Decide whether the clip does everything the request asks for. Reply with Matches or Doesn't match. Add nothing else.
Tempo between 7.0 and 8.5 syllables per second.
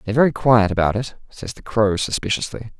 Doesn't match